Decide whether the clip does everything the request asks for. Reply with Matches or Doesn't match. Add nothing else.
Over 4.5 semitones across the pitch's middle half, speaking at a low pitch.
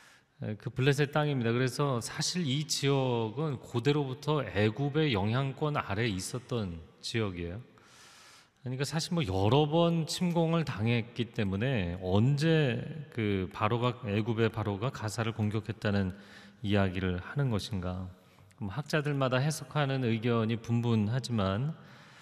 Matches